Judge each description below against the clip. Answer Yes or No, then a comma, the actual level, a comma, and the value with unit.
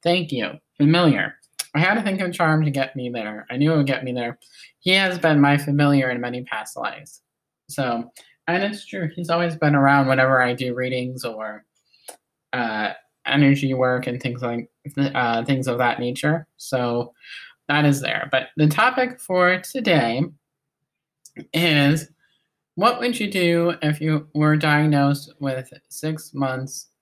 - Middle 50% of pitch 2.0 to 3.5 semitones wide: No, average, 3.9 semitones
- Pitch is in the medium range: Yes, medium, 145 Hz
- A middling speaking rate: Yes, average, 165 wpm